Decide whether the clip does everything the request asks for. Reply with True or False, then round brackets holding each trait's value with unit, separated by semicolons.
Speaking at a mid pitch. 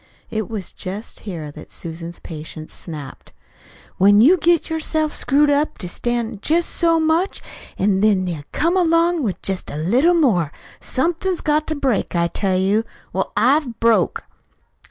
False (230 Hz)